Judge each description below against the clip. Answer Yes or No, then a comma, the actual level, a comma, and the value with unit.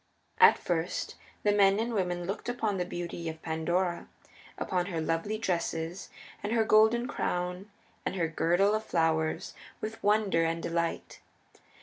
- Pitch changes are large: No, average, 4.1 semitones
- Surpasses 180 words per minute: No, average, 145 wpm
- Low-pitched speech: No, medium, 180 Hz